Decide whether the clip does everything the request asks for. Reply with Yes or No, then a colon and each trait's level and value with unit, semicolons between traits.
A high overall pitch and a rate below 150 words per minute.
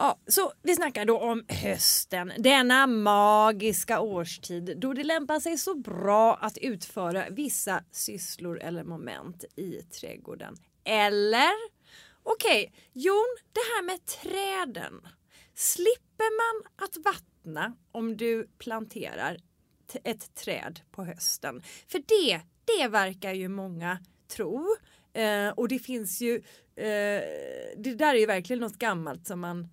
Yes: high, 230 Hz; slow, 125 wpm